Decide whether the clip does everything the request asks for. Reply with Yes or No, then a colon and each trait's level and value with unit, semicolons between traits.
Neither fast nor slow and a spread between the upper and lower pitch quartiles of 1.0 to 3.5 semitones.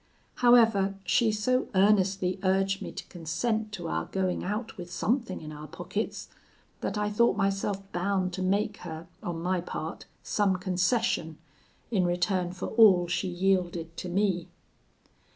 Yes: average, 150 wpm; average, 2.8 semitones